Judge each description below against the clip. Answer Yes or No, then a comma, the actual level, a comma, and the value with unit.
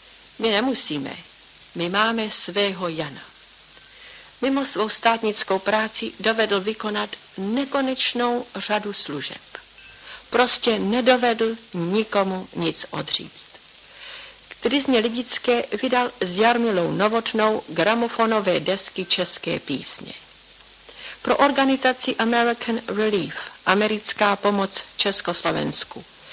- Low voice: No, high, 220 Hz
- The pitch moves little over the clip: No, average, 3.4 semitones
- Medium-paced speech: No, slow, 85 wpm